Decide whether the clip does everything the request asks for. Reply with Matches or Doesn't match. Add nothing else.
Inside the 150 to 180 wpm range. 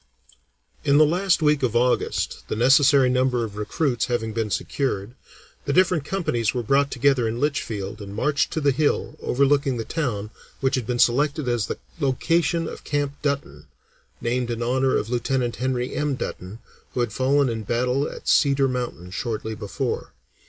Matches